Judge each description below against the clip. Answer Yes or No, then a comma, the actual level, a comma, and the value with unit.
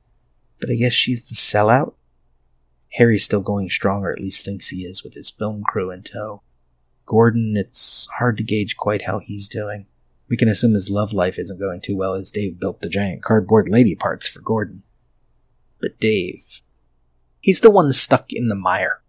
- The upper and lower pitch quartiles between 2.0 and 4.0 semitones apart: Yes, average, 3.5 semitones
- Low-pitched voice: Yes, low, 105 Hz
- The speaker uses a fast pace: No, average, 190 wpm